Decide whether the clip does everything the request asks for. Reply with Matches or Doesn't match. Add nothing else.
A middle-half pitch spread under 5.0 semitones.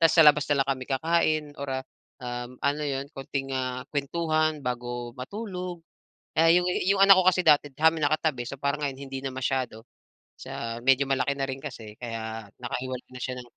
Matches